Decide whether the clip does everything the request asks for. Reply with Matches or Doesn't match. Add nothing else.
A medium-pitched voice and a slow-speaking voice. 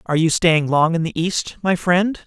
Doesn't match